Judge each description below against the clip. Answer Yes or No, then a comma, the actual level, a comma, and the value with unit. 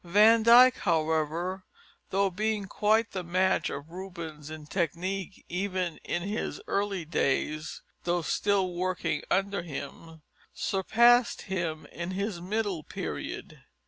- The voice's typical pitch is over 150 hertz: Yes, medium, 185 Hz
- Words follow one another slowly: Yes, slow, 120 wpm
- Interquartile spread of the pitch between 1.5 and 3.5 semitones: Yes, average, 3.2 semitones